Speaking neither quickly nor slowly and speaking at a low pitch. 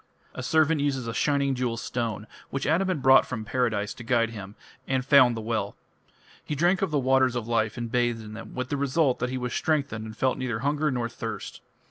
No: fast, 220 wpm; low, 125 Hz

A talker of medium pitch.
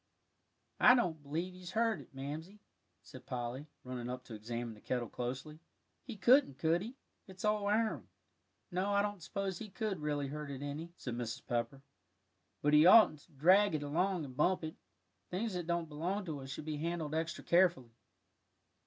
Yes: medium, 160 Hz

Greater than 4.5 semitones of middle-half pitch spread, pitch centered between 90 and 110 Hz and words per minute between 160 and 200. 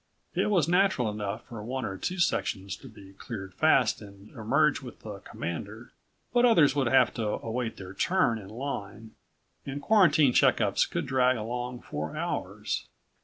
No: average, 5.3 semitones; low, 120 Hz; average, 165 wpm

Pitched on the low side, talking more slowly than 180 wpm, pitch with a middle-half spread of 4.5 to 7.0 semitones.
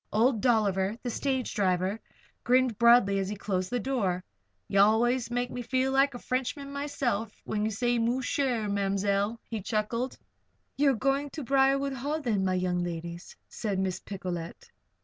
No: high, 230 Hz; average, 165 wpm; average, 4.8 semitones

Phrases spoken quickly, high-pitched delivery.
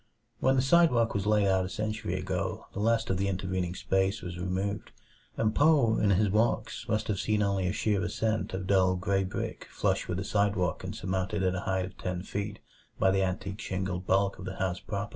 No: fast, 215 wpm; low, 100 Hz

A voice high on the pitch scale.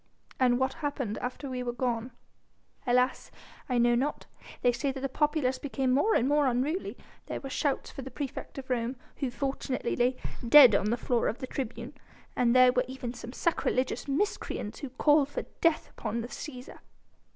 Yes: very high, 255 Hz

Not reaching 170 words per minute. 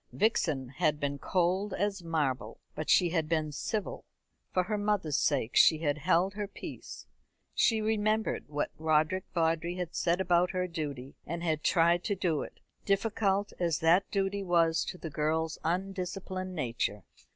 Yes: average, 160 wpm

